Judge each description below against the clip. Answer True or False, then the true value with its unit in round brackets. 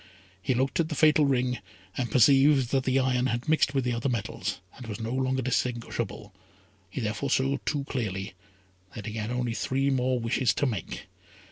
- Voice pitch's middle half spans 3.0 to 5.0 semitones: False (2.6 semitones)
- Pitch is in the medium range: False (125 Hz)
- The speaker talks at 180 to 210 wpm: True (190 wpm)